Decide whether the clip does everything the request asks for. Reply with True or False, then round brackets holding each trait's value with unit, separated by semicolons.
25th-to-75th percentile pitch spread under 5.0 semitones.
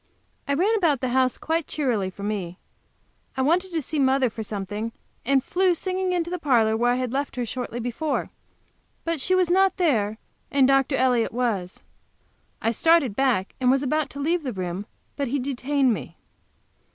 False (5.3 semitones)